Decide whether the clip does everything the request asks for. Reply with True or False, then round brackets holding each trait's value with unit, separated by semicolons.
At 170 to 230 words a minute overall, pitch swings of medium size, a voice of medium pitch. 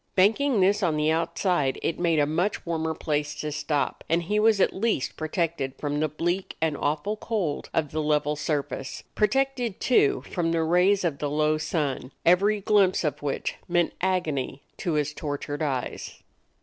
True (175 wpm; 4.1 semitones; 160 Hz)